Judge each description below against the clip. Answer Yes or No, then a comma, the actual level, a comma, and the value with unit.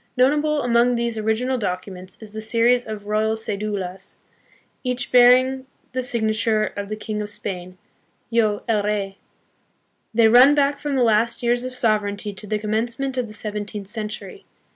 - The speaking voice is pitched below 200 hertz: No, high, 220 Hz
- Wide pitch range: No, average, 2.9 semitones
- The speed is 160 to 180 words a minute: Yes, average, 165 wpm